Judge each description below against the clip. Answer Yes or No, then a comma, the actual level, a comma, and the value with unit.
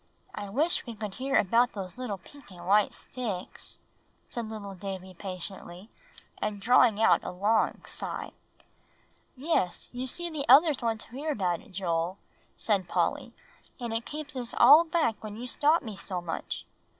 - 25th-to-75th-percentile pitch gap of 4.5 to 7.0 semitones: Yes, average, 5.2 semitones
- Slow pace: No, average, 160 wpm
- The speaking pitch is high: Yes, high, 220 Hz